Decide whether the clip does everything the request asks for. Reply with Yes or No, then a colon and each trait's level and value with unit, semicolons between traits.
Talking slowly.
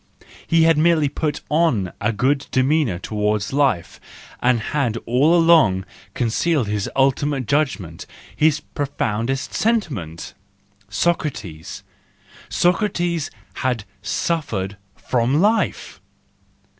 Yes: slow, 95 wpm